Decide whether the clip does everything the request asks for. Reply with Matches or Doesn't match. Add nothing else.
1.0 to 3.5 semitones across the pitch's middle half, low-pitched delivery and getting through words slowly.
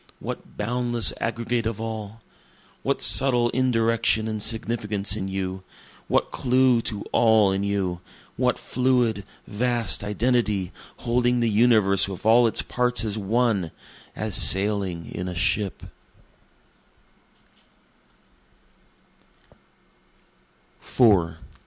Matches